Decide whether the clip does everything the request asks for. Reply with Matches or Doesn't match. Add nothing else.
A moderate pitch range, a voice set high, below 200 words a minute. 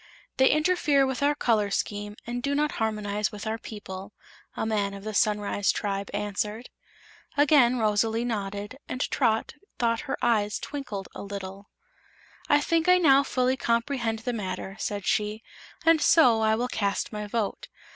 Matches